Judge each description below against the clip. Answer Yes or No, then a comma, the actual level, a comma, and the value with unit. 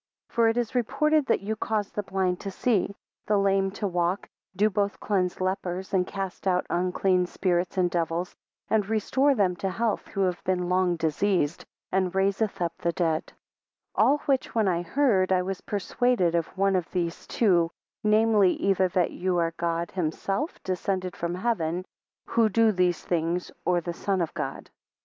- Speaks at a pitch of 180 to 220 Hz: Yes, high, 190 Hz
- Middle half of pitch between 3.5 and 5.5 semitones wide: No, average, 2.8 semitones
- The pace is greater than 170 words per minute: Yes, average, 180 wpm